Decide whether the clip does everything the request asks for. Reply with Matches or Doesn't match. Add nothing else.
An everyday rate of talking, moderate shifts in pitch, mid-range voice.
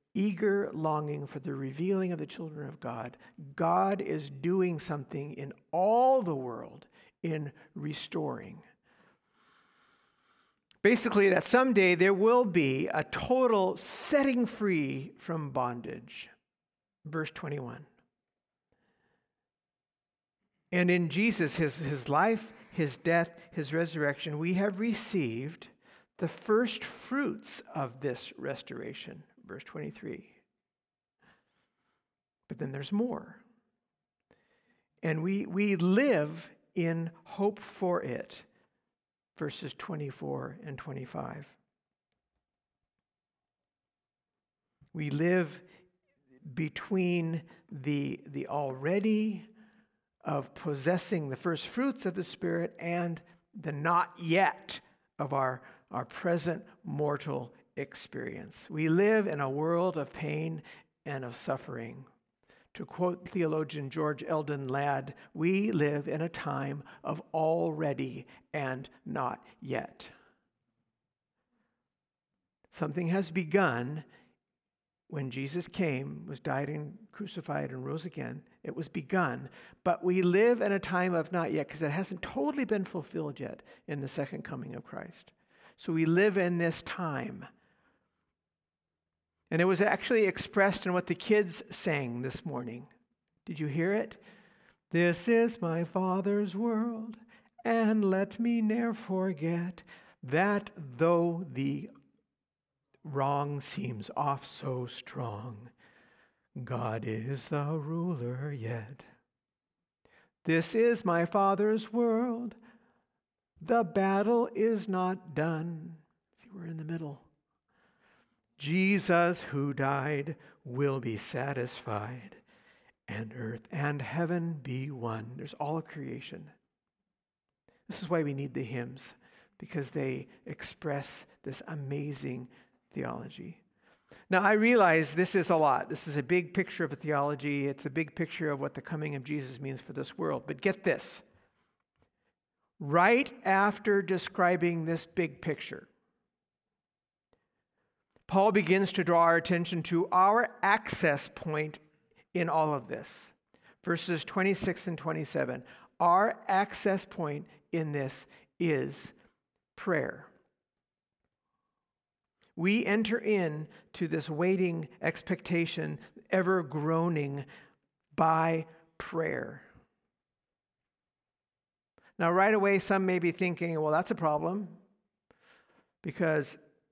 Doesn't match